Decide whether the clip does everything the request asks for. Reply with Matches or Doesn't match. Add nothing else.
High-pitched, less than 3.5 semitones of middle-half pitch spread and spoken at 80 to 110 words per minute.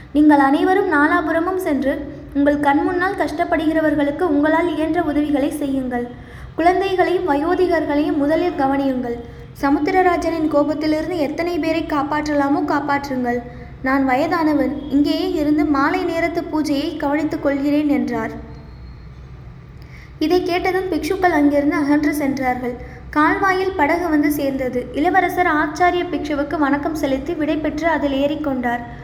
Matches